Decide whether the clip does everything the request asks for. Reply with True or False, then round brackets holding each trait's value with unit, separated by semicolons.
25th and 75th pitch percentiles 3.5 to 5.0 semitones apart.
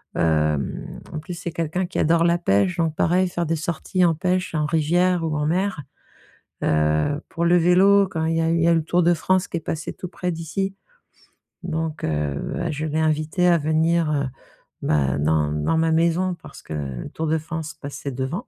False (2.7 semitones)